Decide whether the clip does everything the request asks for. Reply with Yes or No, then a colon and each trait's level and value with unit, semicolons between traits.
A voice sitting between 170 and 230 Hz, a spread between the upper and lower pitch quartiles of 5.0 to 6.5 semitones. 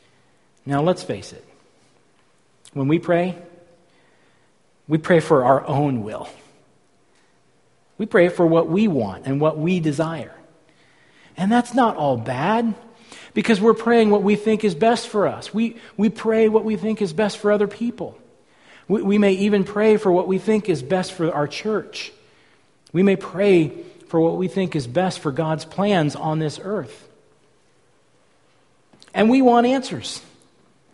Yes: medium, 185 Hz; average, 5.3 semitones